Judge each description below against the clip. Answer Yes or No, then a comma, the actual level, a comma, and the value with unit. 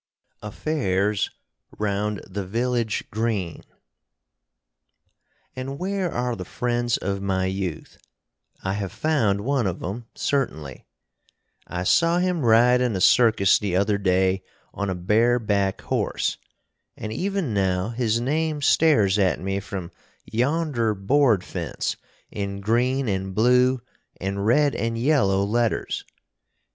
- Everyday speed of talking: No, slow, 125 wpm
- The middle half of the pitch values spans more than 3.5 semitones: Yes, average, 4.4 semitones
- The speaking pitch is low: Yes, low, 110 Hz